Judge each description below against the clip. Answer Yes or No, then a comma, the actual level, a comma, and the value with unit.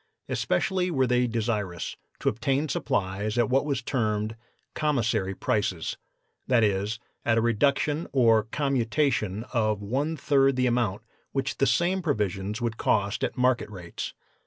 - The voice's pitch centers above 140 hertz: No, low, 120 Hz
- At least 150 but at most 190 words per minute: No, average, 140 wpm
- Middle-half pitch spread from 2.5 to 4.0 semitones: No, average, 4.5 semitones